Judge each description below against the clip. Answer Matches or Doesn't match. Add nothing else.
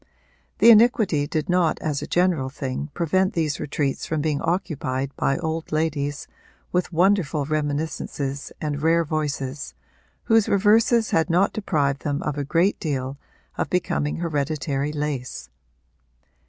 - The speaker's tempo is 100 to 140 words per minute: Matches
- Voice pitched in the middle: Matches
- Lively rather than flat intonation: Doesn't match